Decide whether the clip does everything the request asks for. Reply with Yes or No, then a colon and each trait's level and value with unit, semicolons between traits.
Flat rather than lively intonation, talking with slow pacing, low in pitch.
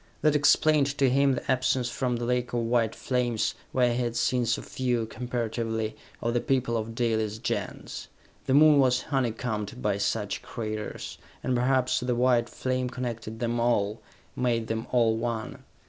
No: narrow, 2.1 semitones; average, 165 wpm; low, 120 Hz